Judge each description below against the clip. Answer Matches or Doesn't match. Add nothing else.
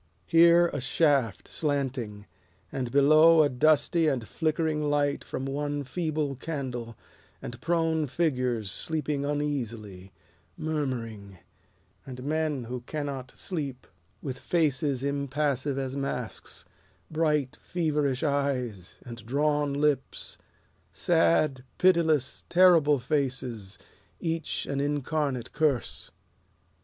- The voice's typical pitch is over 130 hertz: Matches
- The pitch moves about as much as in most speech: Matches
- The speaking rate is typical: Doesn't match